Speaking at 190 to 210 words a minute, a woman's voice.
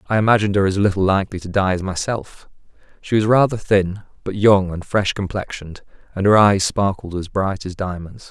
No: average, 195 wpm; male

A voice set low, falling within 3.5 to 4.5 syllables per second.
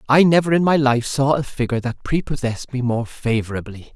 No: low, 130 Hz; 5.8 syllables/s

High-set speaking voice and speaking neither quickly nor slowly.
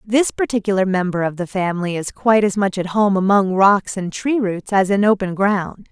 No: high, 195 Hz; fast, 215 wpm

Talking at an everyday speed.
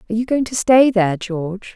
No: fast, 240 wpm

